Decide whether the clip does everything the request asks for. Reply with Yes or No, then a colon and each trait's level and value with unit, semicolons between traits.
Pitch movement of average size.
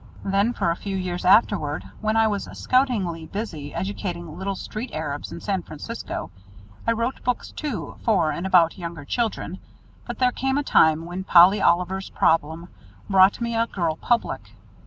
Yes: average, 4.8 semitones